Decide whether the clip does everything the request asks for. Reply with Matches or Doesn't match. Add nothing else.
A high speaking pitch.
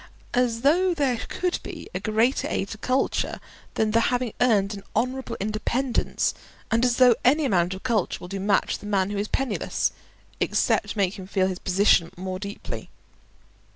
Matches